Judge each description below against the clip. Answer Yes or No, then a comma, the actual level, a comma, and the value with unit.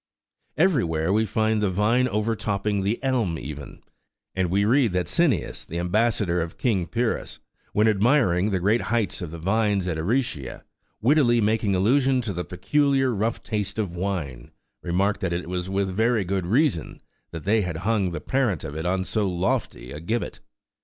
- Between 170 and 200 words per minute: Yes, average, 175 wpm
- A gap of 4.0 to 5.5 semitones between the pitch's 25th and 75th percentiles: Yes, average, 4.3 semitones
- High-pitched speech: No, low, 100 Hz